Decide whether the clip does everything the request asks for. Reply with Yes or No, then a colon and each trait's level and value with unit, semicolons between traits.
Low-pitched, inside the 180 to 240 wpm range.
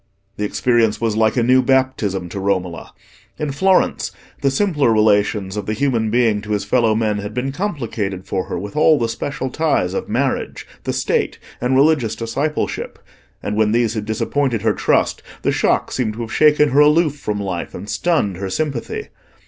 Yes: low, 115 Hz; average, 185 wpm